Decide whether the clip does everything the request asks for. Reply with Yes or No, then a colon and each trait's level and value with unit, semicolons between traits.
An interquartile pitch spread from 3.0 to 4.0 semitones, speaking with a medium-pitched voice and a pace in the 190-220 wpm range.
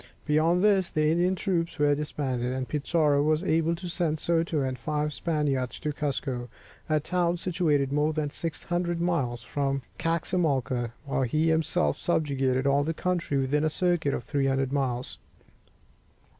No: average, 3.5 semitones; medium, 150 Hz; average, 150 wpm